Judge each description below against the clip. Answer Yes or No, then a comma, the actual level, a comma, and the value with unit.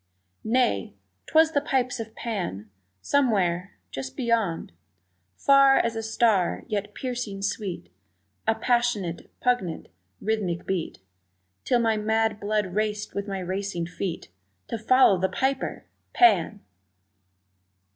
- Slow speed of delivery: Yes, slow, 115 wpm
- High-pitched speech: Yes, high, 210 Hz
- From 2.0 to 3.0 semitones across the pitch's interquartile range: No, average, 4.4 semitones